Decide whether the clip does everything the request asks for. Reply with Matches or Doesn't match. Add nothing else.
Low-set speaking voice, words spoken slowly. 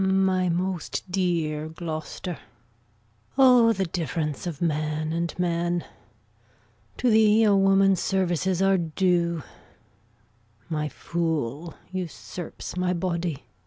Doesn't match